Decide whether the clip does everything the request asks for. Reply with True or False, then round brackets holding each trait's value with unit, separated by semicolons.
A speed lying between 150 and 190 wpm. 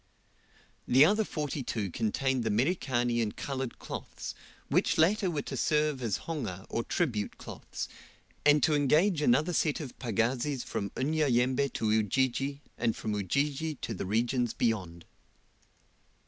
False (140 wpm)